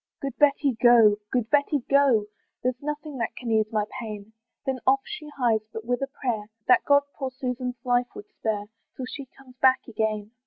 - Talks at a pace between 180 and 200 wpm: Yes, average, 190 wpm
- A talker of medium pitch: No, very high, 250 Hz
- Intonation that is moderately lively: Yes, average, 3.6 semitones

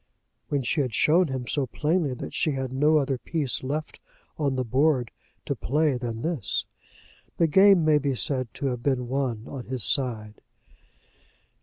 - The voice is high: No, low, 135 Hz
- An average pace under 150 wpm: No, average, 170 wpm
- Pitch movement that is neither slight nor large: Yes, average, 3.4 semitones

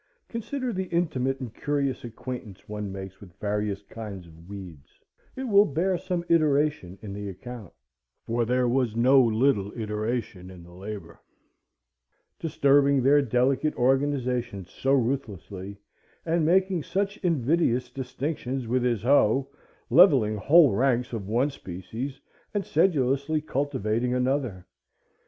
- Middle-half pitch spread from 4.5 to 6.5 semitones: Yes, wide, 5.5 semitones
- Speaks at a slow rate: Yes, slow, 125 wpm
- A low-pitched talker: Yes, low, 125 Hz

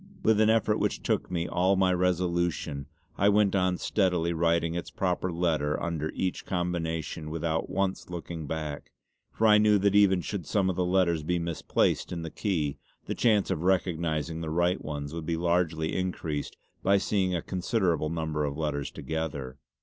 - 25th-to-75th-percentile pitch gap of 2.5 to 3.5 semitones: Yes, average, 2.8 semitones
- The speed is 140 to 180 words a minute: Yes, average, 175 wpm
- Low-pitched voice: Yes, very low, 85 Hz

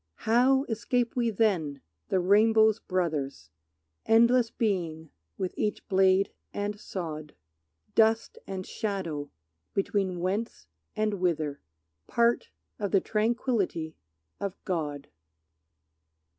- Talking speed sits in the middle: No, slow, 100 wpm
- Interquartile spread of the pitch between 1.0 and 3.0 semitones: No, average, 4.8 semitones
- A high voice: Yes, high, 195 Hz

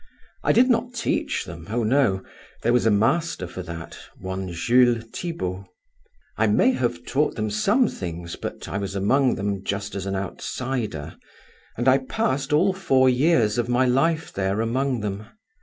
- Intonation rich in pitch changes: Yes, wide, 5.7 semitones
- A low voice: Yes, low, 120 Hz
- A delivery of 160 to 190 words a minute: Yes, average, 170 wpm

